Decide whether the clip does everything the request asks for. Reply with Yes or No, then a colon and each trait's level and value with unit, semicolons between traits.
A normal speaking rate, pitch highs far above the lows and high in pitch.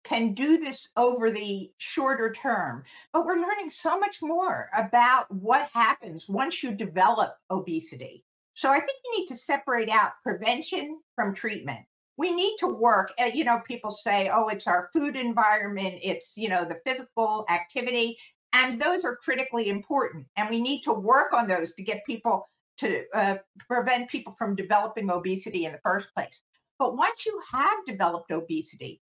Yes: average, 170 wpm; wide, 5.9 semitones; high, 235 Hz